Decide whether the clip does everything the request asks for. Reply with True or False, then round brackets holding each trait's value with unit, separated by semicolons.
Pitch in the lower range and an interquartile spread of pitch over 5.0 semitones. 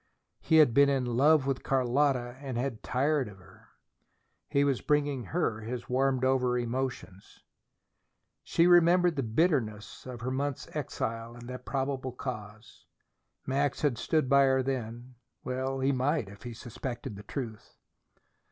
False (130 Hz; 2.8 semitones)